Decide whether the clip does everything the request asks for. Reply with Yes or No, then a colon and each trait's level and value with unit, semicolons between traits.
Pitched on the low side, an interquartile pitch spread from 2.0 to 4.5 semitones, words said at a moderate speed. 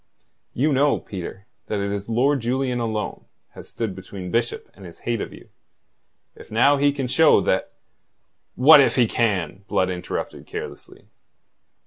No: low, 115 Hz; average, 5.2 semitones; average, 155 wpm